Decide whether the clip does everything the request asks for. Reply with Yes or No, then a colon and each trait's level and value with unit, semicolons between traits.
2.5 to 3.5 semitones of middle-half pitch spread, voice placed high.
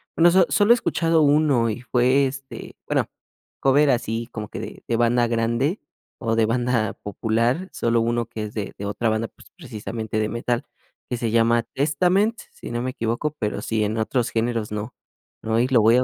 No: average, 3.1 semitones; low, 120 Hz